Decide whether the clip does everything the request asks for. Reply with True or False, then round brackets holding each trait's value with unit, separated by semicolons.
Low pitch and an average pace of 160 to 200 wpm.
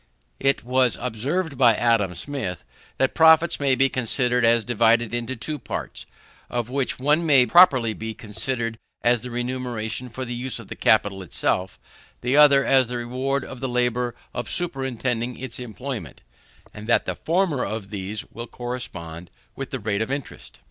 True (125 Hz; 170 wpm)